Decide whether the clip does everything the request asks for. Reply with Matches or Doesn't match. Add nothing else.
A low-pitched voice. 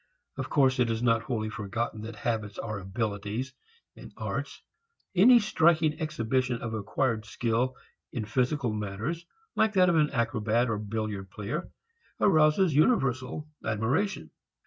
Matches